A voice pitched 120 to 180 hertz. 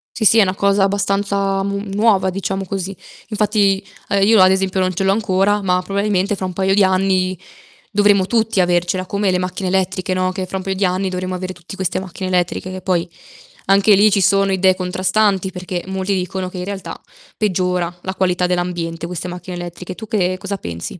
No: high, 190 Hz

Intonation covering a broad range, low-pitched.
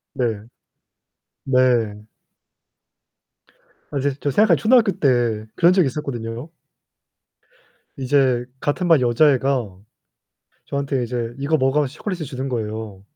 No: average, 3.7 semitones; low, 130 Hz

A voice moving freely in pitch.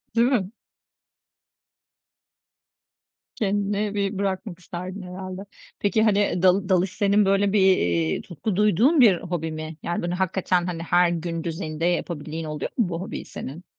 No: average, 2.9 semitones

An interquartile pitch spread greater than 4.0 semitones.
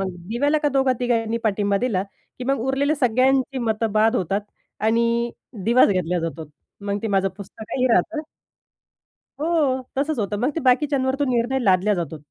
Yes: average, 4.7 semitones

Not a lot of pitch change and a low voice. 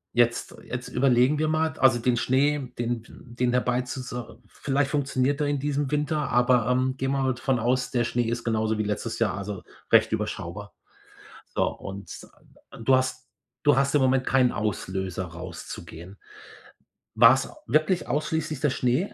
No: average, 3.0 semitones; low, 125 Hz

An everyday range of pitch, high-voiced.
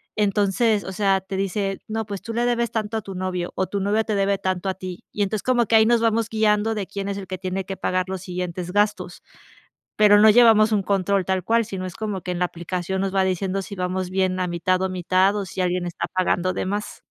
No: narrow, 2.2 semitones; high, 195 Hz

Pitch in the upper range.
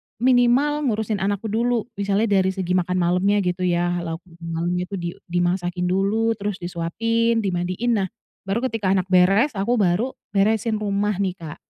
Yes: high, 195 Hz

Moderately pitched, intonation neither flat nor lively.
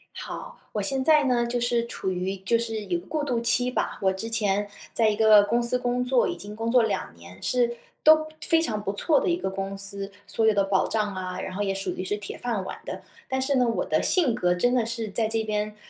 No: high, 220 Hz; average, 3.7 semitones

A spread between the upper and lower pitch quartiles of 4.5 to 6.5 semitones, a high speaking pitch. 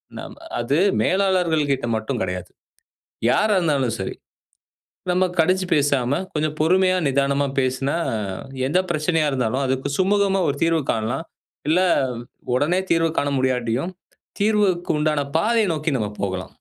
No: wide, 5.6 semitones; medium, 150 Hz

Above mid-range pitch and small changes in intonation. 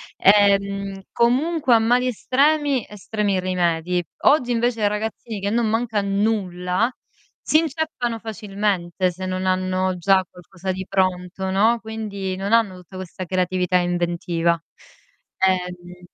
No: high, 195 Hz; average, 3.6 semitones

